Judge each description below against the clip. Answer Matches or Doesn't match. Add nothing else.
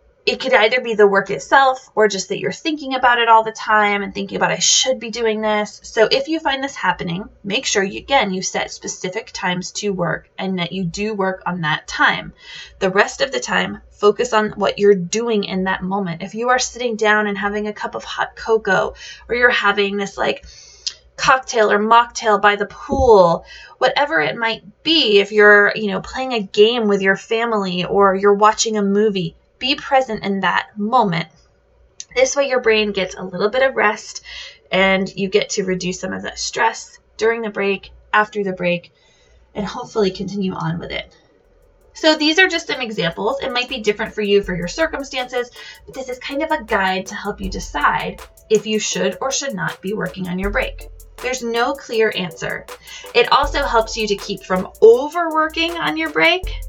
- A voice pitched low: Doesn't match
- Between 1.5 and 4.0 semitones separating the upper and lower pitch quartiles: Doesn't match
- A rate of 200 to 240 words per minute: Matches